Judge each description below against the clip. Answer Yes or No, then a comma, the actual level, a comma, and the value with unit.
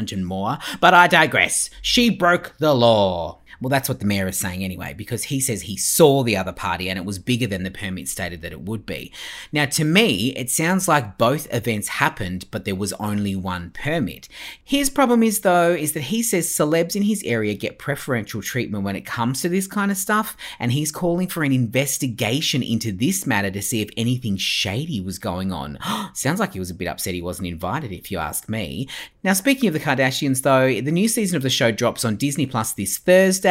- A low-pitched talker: Yes, low, 125 Hz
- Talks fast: Yes, fast, 220 wpm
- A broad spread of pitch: Yes, wide, 8.5 semitones